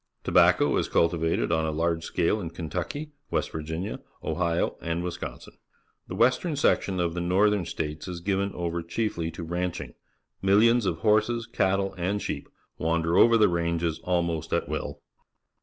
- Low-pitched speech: Yes, very low, 85 Hz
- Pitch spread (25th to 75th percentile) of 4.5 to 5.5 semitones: No, average, 3.1 semitones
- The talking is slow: No, average, 145 wpm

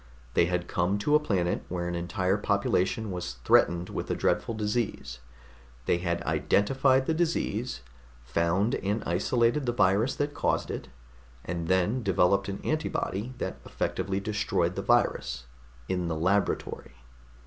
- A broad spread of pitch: No, average, 4.4 semitones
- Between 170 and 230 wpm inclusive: No, average, 145 wpm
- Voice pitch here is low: Yes, very low, 95 Hz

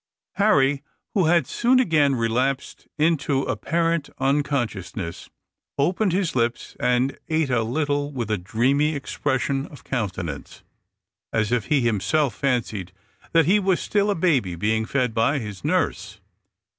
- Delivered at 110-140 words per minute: Yes, slow, 135 wpm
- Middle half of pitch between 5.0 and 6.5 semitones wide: Yes, wide, 5.4 semitones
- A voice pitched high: No, low, 135 Hz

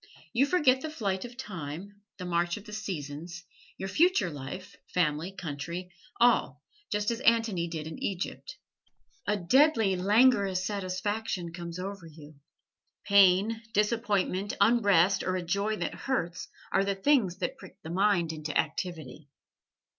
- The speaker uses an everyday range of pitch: Yes, average, 3.8 semitones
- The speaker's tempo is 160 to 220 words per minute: No, average, 140 wpm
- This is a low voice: No, high, 190 Hz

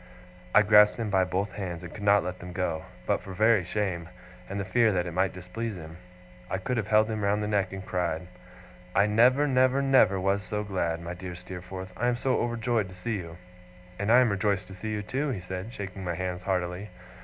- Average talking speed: No, fast, 225 wpm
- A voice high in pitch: No, low, 100 Hz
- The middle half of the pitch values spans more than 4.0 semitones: No, average, 3.0 semitones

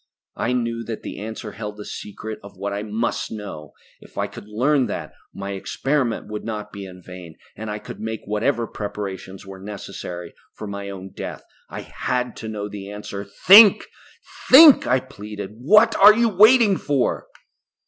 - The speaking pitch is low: Yes, low, 105 Hz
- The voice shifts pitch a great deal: No, average, 3.9 semitones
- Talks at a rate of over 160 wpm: Yes, average, 175 wpm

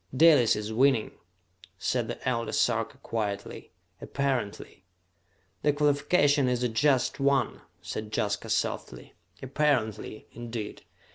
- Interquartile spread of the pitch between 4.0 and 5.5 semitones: Yes, average, 4.3 semitones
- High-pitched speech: No, low, 125 Hz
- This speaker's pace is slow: Yes, slow, 110 wpm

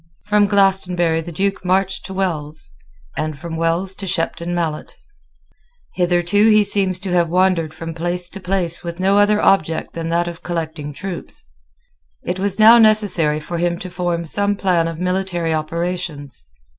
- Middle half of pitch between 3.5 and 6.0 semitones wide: No, average, 2.7 semitones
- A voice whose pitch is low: No, medium, 175 Hz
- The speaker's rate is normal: Yes, average, 160 wpm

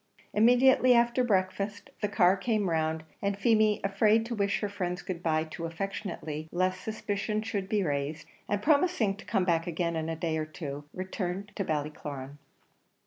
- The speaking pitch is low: No, high, 195 Hz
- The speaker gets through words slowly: No, average, 170 wpm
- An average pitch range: Yes, average, 4.6 semitones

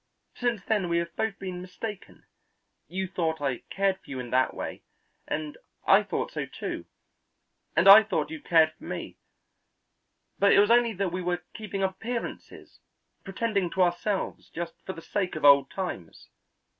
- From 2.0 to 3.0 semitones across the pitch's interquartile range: No, average, 3.4 semitones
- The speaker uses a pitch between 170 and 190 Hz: Yes, medium, 185 Hz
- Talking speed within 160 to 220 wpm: Yes, average, 170 wpm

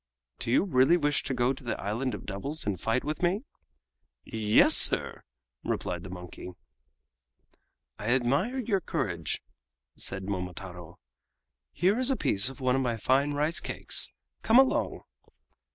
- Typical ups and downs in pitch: No, wide, 7.5 semitones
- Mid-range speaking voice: No, low, 130 Hz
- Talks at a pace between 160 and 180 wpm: No, average, 150 wpm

